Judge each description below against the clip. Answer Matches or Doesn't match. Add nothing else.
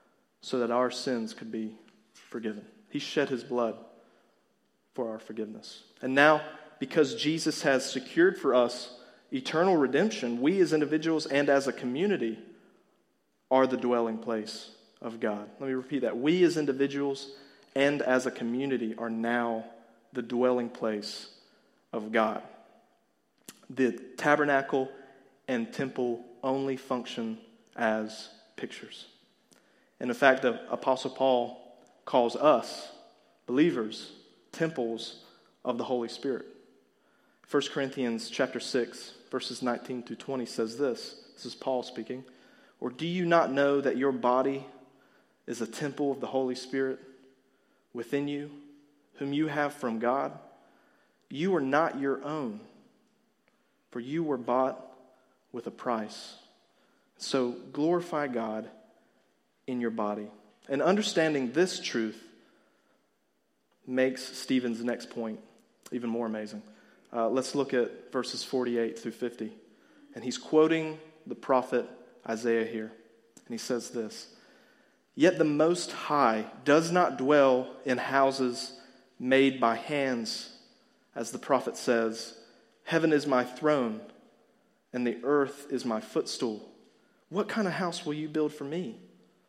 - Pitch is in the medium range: Doesn't match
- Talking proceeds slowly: Matches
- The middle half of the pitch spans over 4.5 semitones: Doesn't match